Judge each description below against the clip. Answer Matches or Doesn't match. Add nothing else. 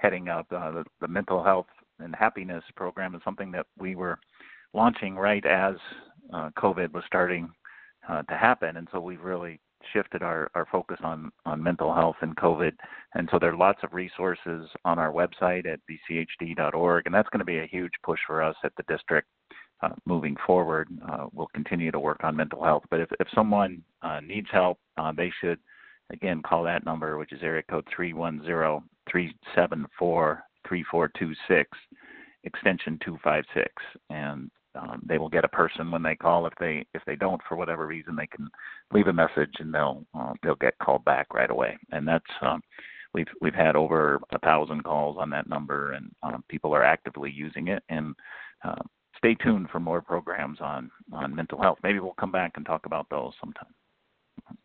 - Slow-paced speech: Doesn't match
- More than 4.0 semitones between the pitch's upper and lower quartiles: Doesn't match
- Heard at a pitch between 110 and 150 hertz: Doesn't match